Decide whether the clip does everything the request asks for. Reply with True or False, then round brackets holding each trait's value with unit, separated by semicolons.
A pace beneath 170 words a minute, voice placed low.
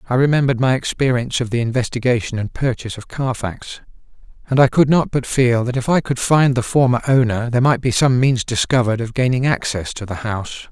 False (205 wpm; 125 Hz)